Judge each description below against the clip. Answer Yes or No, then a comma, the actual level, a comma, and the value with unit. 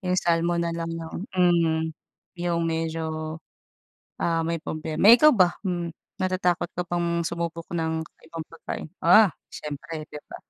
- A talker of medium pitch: Yes, medium, 165 Hz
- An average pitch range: No, narrow, 1.4 semitones